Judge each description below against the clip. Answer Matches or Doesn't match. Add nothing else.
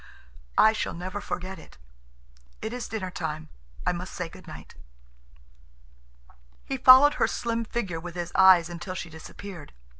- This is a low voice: Doesn't match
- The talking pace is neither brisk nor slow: Matches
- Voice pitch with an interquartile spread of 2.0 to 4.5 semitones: Matches